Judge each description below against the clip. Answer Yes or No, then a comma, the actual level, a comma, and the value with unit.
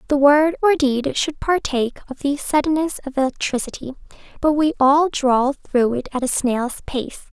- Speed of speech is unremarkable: Yes, average, 170 wpm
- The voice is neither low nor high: No, very high, 280 Hz